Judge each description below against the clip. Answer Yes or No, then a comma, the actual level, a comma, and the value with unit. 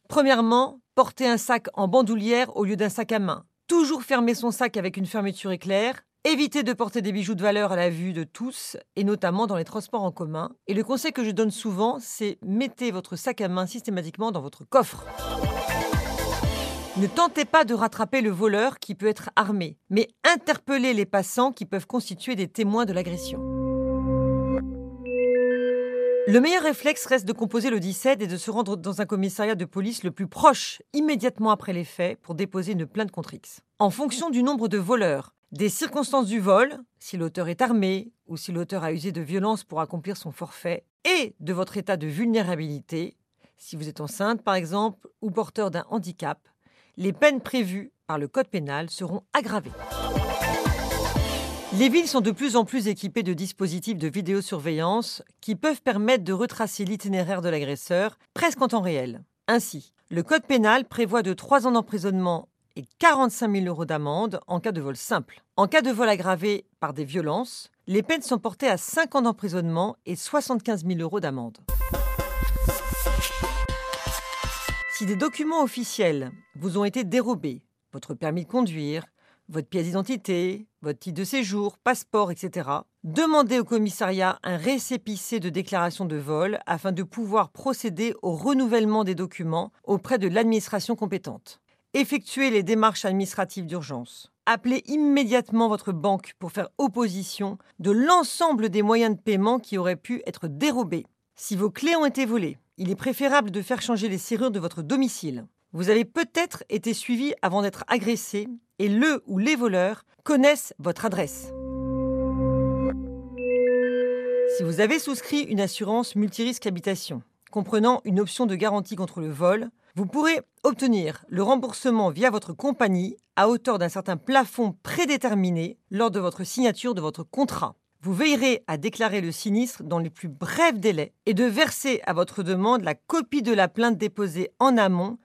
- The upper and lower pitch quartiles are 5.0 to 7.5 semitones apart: Yes, average, 5.3 semitones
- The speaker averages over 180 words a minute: No, average, 170 wpm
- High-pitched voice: Yes, high, 210 Hz